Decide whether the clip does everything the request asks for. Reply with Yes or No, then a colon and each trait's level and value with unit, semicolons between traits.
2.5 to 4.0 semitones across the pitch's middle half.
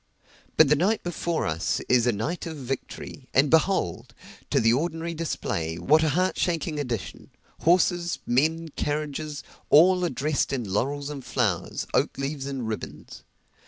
No: average, 4.5 semitones